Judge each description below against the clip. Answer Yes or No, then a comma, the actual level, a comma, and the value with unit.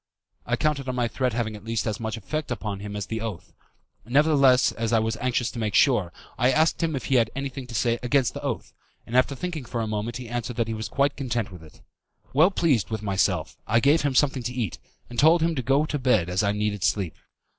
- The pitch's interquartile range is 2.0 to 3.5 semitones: No, average, 3.9 semitones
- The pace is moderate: No, fast, 240 wpm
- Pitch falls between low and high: No, low, 120 Hz